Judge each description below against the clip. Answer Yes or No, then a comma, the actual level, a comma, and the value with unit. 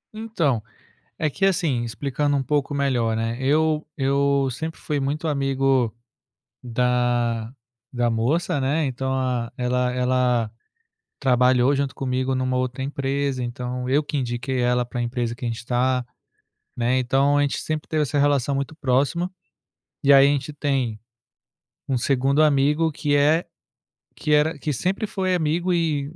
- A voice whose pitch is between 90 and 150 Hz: Yes, low, 135 Hz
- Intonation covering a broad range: No, average, 2.8 semitones